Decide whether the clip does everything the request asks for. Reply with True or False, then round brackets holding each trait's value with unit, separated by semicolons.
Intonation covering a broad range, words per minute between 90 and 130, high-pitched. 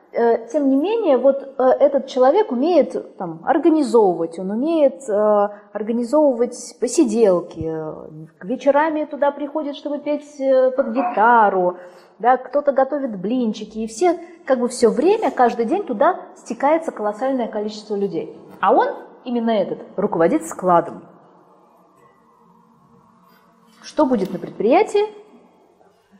True (5.8 semitones; 110 wpm; 250 Hz)